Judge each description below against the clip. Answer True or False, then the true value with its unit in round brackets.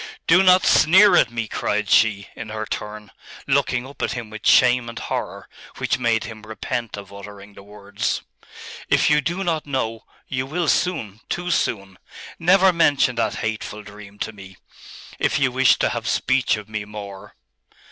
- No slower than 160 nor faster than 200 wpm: True (175 wpm)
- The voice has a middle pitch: False (110 Hz)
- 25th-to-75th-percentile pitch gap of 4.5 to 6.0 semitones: True (5.0 semitones)